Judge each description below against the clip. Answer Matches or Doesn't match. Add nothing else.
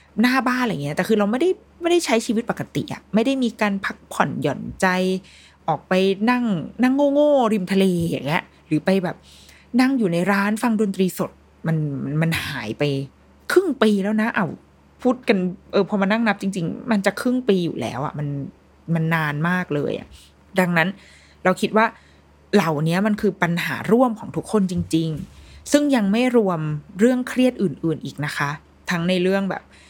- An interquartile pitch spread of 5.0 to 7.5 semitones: Matches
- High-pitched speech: Matches